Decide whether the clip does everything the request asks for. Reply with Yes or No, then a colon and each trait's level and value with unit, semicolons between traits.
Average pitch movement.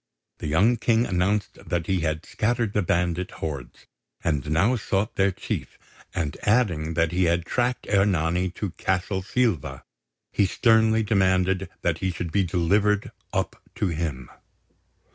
Yes: average, 3.8 semitones